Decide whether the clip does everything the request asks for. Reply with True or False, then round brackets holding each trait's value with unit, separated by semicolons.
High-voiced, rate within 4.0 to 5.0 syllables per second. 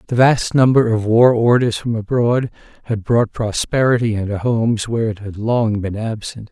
False (115 Hz; 4.9 syllables/s)